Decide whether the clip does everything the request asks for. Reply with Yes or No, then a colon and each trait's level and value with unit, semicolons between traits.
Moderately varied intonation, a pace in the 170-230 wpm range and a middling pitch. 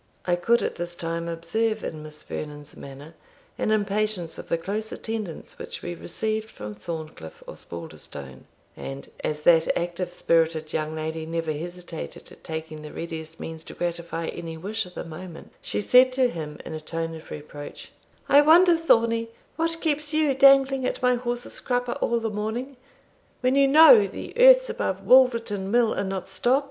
No: wide, 7.2 semitones; average, 175 wpm; medium, 180 Hz